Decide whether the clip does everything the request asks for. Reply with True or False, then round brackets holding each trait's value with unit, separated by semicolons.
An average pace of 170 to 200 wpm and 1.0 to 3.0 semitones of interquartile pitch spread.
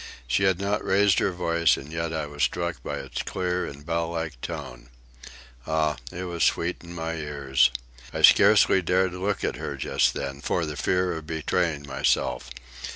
False (180 wpm; 3.6 semitones)